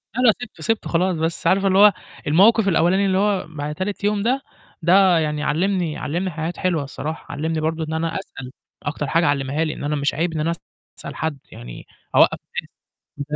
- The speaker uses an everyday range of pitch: Yes, average, 4.0 semitones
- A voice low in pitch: No, medium, 165 Hz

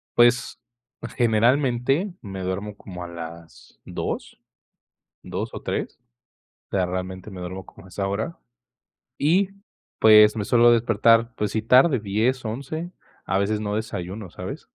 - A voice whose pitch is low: Yes, low, 110 Hz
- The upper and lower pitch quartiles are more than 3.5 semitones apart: Yes, average, 4.0 semitones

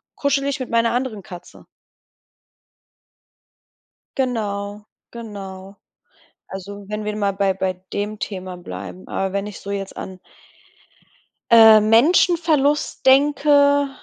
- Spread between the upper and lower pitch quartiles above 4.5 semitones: Yes, wide, 5.4 semitones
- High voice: Yes, high, 210 Hz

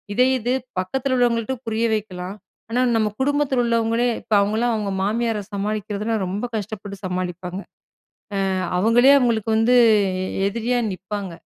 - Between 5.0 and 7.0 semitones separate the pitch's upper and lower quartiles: No, average, 3.2 semitones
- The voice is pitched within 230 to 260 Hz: No, high, 220 Hz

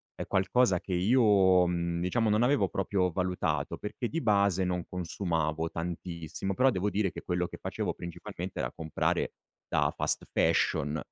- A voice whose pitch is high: No, very low, 90 Hz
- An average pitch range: Yes, average, 3.1 semitones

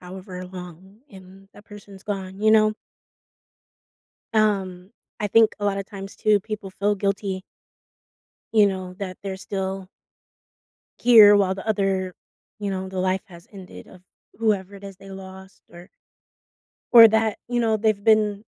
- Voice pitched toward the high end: Yes, high, 195 Hz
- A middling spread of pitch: No, narrow, 1.9 semitones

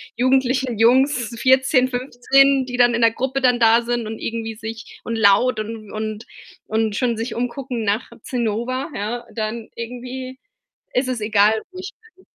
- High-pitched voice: Yes, high, 240 Hz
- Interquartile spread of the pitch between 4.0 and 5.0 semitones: No, narrow, 2.5 semitones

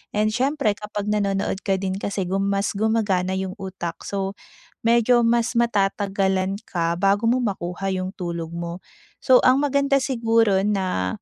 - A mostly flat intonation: No, average, 3.3 semitones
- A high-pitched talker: Yes, high, 195 Hz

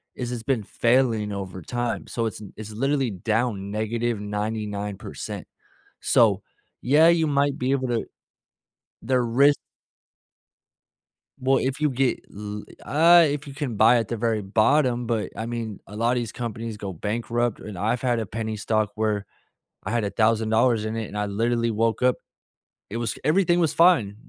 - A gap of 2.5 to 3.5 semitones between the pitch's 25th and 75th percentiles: Yes, average, 3.1 semitones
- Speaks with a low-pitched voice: Yes, low, 115 Hz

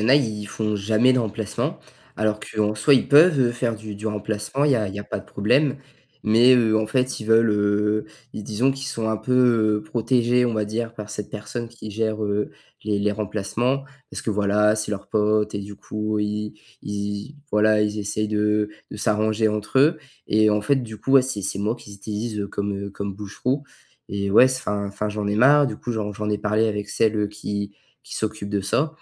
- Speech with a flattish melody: Yes, narrow, 2.1 semitones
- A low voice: Yes, low, 105 Hz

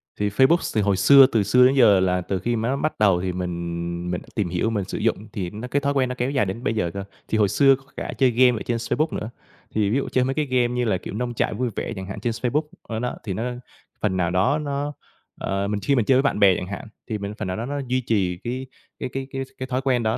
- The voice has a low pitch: Yes, low, 115 Hz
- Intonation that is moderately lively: Yes, average, 4.9 semitones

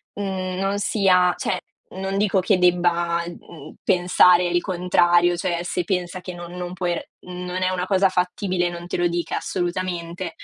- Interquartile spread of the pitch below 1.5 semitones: Yes, narrow, 1.1 semitones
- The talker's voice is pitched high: No, medium, 180 Hz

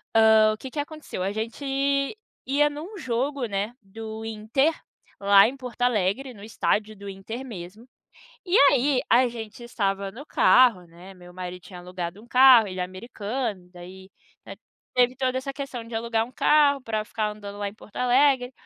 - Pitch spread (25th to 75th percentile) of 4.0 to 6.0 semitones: Yes, average, 4.6 semitones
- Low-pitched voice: No, high, 225 Hz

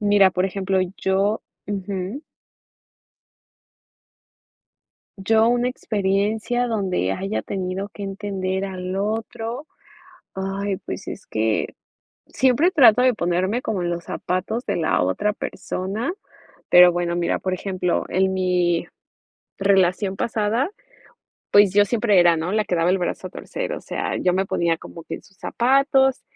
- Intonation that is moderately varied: Yes, average, 3.1 semitones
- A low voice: No, high, 195 Hz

